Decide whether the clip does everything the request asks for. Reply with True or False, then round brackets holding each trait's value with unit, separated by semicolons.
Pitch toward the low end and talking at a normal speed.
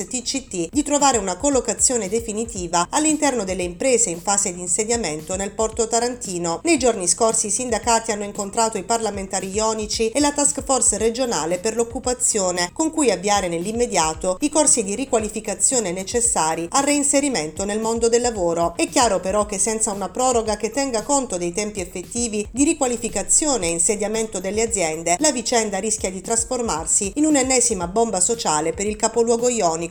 False (225 Hz; 160 wpm)